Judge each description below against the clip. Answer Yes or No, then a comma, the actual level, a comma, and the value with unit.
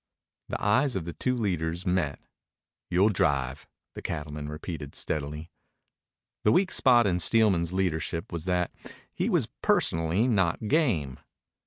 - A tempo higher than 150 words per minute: No, slow, 135 wpm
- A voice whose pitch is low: Yes, very low, 85 Hz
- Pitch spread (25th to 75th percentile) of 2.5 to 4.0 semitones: No, average, 5.0 semitones